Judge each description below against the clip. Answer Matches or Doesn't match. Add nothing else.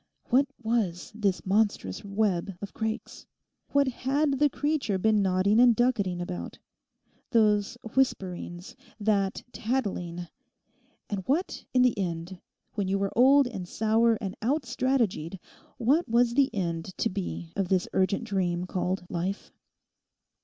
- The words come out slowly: Matches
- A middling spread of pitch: Matches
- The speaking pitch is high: Matches